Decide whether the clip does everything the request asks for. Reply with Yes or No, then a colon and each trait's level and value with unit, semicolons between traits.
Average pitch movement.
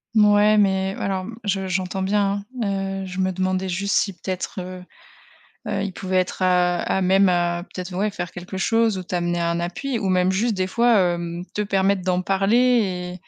No: narrow, 1.7 semitones